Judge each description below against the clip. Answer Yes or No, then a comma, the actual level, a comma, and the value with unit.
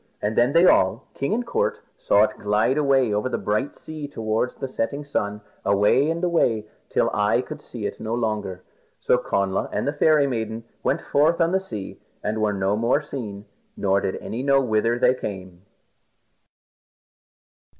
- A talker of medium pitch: No, low, 120 Hz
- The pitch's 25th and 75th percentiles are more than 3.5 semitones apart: Yes, wide, 5.5 semitones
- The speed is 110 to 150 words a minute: No, average, 180 wpm